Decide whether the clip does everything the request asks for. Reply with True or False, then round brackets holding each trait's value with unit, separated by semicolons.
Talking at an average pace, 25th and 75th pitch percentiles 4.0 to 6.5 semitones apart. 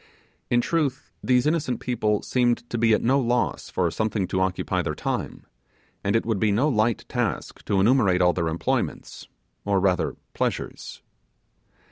True (160 wpm; 4.3 semitones)